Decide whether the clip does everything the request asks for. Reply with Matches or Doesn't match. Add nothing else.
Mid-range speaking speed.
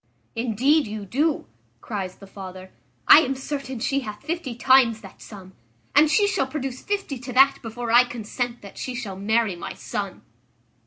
Matches